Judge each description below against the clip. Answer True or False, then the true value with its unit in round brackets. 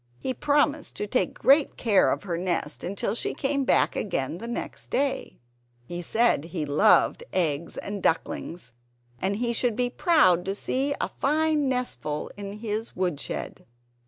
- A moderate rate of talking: True (155 wpm)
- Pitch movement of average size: False (7.0 semitones)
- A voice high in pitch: True (210 Hz)